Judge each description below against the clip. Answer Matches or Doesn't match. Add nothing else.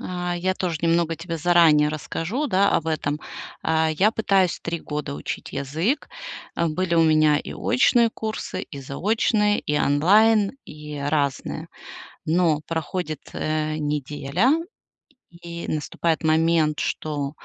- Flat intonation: Doesn't match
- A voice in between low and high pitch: Matches